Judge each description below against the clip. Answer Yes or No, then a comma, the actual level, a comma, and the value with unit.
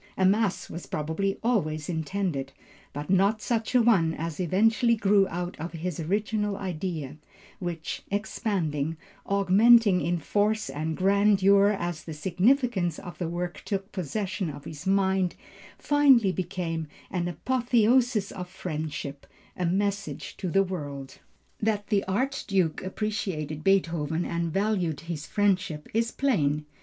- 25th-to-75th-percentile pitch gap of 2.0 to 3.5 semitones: No, average, 4.1 semitones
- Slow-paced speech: Yes, slow, 130 wpm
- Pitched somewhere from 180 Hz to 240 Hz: Yes, medium, 185 Hz